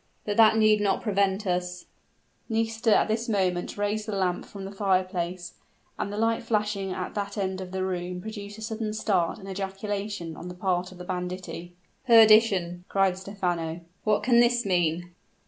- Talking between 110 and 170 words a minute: No, average, 180 wpm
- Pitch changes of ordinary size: Yes, average, 3.0 semitones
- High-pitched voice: Yes, high, 195 Hz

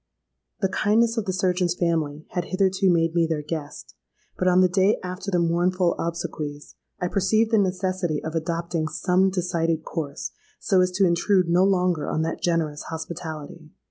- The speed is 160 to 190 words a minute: Yes, average, 170 wpm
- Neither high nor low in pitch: Yes, medium, 175 Hz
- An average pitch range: No, narrow, 2.2 semitones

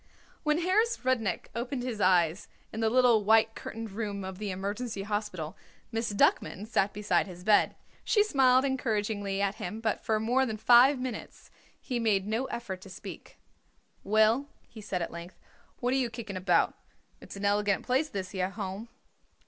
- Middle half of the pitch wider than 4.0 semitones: No, average, 3.6 semitones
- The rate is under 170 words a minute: No, average, 175 wpm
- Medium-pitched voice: No, high, 215 Hz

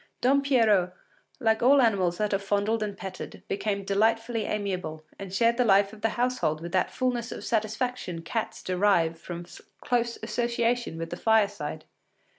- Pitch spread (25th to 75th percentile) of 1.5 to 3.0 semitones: No, average, 4.1 semitones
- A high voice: Yes, high, 210 Hz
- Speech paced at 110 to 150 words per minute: No, average, 160 wpm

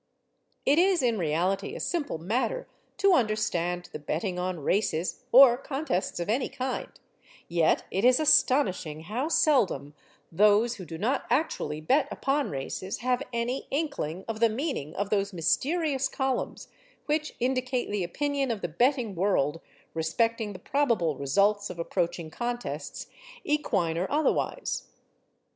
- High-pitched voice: Yes, high, 220 Hz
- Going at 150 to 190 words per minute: No, average, 140 wpm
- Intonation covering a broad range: Yes, wide, 7.3 semitones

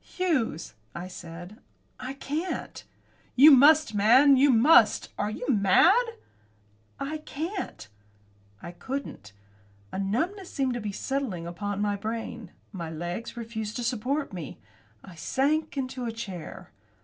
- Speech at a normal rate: No, slow, 130 wpm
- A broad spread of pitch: Yes, wide, 6.2 semitones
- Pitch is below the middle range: No, high, 235 Hz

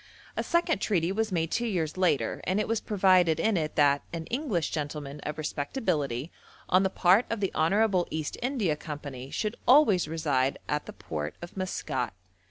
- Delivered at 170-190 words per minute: Yes, average, 180 wpm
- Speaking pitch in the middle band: Yes, medium, 170 Hz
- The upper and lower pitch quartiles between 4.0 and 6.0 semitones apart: Yes, wide, 5.5 semitones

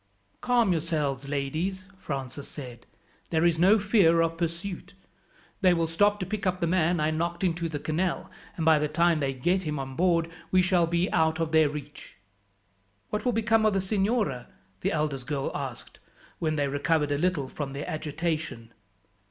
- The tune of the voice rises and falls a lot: No, average, 3.9 semitones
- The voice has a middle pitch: Yes, medium, 165 Hz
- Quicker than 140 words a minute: Yes, average, 180 wpm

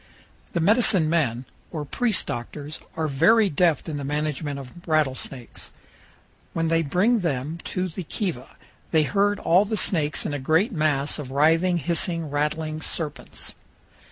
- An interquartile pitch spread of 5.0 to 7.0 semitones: No, average, 3.5 semitones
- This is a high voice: No, medium, 160 Hz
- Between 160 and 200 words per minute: No, average, 150 wpm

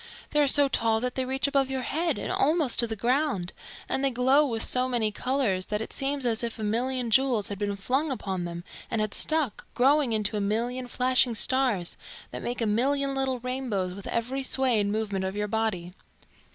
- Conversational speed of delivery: No, fast, 210 wpm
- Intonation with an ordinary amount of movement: Yes, average, 4.0 semitones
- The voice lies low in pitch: No, high, 245 Hz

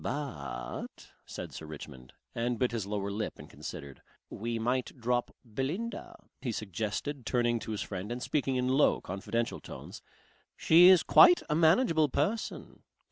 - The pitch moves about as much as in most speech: No, wide, 6.2 semitones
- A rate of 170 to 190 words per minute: No, average, 150 wpm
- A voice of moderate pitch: No, low, 120 Hz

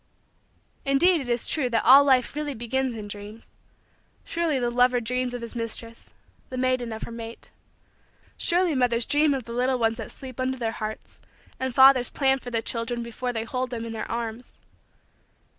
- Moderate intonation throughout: No, narrow, 2.3 semitones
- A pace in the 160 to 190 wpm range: Yes, average, 185 wpm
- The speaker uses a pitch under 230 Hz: No, high, 245 Hz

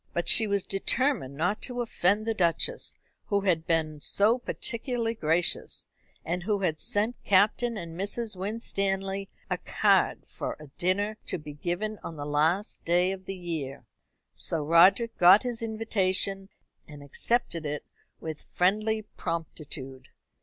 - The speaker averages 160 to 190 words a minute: No, average, 145 wpm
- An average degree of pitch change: Yes, average, 4.7 semitones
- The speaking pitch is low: No, high, 190 Hz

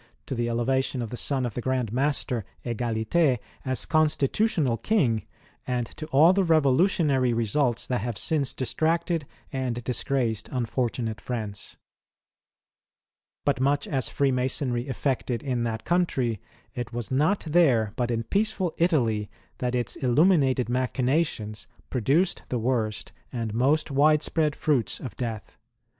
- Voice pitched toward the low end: Yes, low, 130 Hz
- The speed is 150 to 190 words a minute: No, slow, 135 wpm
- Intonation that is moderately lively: Yes, average, 4.0 semitones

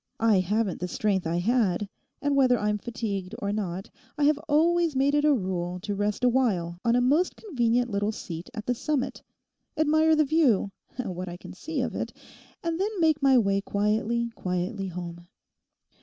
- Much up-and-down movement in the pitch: Yes, wide, 6.6 semitones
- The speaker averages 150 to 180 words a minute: Yes, average, 170 wpm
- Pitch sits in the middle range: No, high, 225 Hz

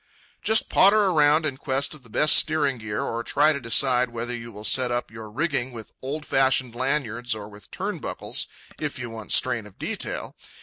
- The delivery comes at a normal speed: Yes, average, 190 wpm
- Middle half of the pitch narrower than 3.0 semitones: No, average, 4.1 semitones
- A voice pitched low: Yes, low, 125 Hz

